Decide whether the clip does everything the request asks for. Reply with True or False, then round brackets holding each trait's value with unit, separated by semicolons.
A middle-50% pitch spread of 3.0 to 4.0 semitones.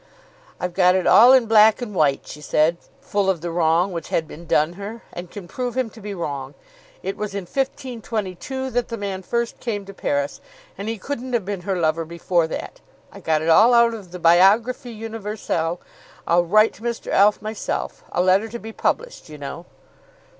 False (4.8 semitones)